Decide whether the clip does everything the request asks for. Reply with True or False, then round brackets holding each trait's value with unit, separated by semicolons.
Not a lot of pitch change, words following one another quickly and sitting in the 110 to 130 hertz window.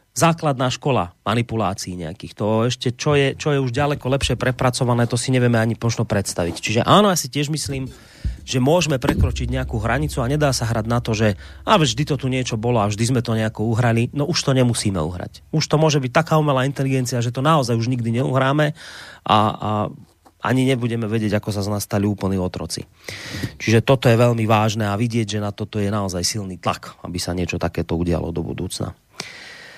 False (4.5 semitones; 205 wpm; 120 Hz)